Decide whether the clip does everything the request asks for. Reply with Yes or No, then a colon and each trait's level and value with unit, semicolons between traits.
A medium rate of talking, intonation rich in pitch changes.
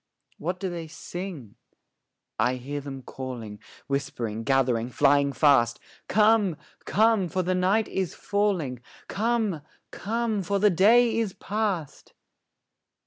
No: slow, 120 wpm; wide, 7.3 semitones